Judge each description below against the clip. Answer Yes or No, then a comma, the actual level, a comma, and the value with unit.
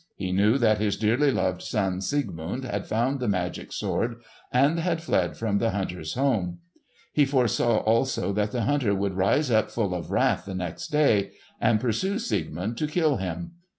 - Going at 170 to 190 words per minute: Yes, average, 180 wpm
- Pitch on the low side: Yes, low, 110 Hz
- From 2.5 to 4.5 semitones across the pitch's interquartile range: No, wide, 5.6 semitones